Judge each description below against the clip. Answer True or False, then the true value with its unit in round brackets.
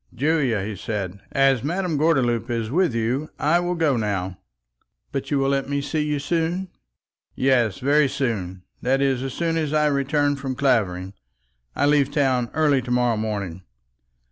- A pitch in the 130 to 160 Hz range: True (135 Hz)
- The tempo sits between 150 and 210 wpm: True (170 wpm)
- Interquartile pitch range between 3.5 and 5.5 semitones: True (4.5 semitones)